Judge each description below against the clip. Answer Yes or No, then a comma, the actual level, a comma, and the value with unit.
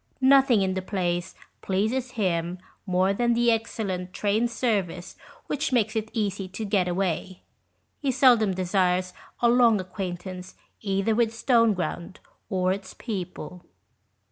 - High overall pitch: Yes, high, 195 Hz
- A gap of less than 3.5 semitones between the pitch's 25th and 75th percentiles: No, average, 3.8 semitones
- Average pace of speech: No, slow, 130 wpm